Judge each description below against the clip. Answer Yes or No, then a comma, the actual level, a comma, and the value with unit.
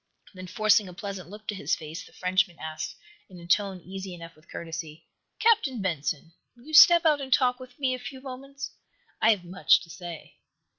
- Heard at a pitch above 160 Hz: Yes, high, 190 Hz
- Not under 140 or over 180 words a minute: No, average, 200 wpm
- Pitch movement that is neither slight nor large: No, wide, 6.7 semitones